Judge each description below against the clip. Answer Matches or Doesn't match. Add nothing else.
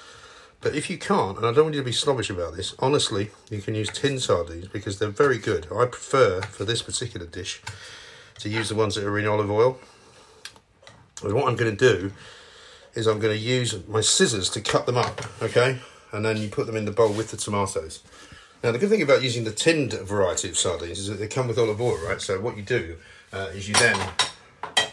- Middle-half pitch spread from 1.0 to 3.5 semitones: Matches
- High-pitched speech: Doesn't match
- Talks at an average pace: Doesn't match